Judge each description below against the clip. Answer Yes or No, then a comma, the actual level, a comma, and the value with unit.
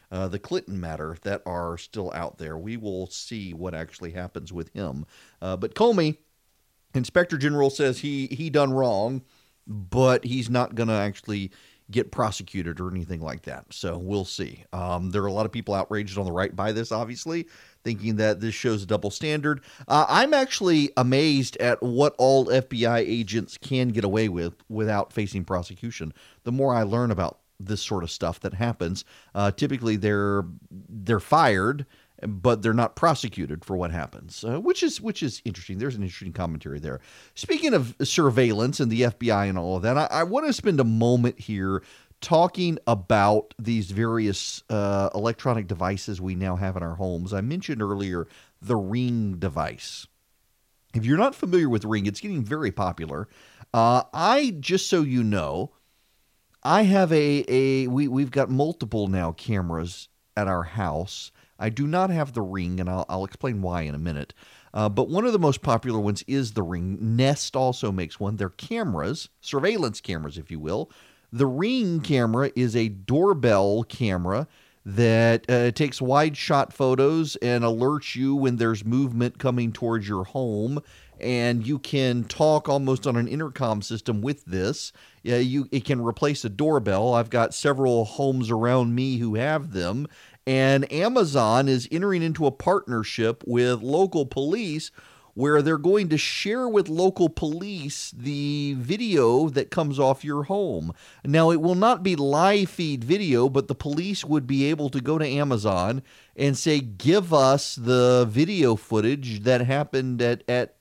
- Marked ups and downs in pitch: Yes, wide, 5.9 semitones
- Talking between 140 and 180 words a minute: Yes, average, 170 wpm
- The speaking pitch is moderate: No, low, 120 Hz